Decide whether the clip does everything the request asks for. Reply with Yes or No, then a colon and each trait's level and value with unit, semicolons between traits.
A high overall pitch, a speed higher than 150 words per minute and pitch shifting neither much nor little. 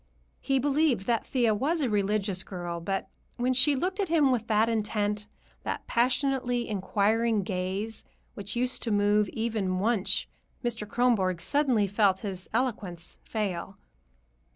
No: high, 215 Hz; average, 140 wpm; average, 4.0 semitones